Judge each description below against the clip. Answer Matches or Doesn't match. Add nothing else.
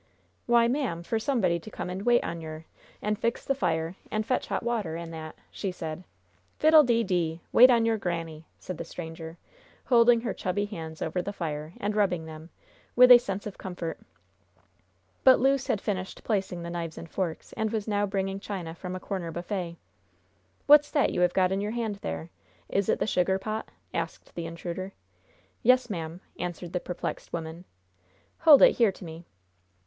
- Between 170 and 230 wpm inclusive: Matches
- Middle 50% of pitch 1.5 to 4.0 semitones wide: Doesn't match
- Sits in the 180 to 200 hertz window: Matches